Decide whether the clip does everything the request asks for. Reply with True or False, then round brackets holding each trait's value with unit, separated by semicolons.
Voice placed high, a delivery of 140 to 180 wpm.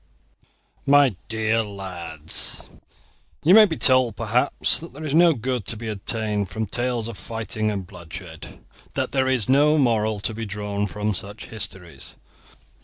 False (110 Hz; 155 wpm)